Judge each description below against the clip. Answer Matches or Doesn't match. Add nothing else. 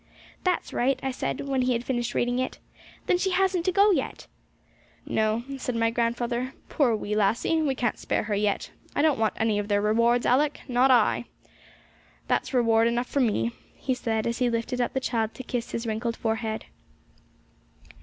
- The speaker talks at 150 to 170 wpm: Doesn't match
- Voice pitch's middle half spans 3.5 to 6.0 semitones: Doesn't match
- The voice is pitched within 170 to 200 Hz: Doesn't match